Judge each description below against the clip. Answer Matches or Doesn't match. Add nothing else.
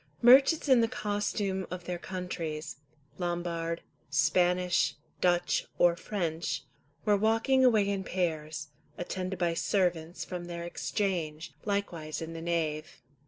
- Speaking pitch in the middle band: Matches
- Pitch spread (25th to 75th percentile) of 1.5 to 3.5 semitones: Matches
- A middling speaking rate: Doesn't match